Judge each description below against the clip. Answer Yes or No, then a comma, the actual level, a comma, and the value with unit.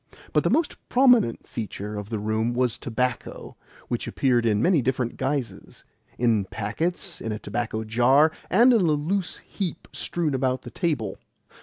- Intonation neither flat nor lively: No, wide, 6.6 semitones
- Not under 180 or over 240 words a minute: No, average, 160 wpm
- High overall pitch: No, low, 125 Hz